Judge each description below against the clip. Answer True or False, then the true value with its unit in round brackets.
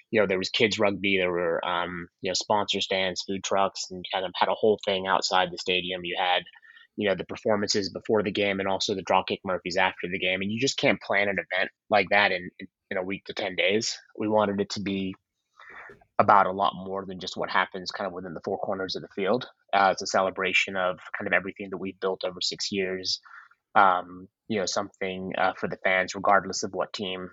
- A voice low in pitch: True (95 Hz)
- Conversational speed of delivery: False (235 wpm)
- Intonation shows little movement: True (1.5 semitones)